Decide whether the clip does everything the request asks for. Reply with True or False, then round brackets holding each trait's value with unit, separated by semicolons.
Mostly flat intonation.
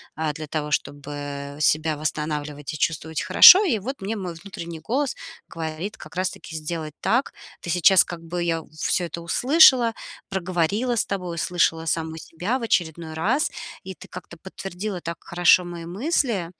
False (3.7 semitones)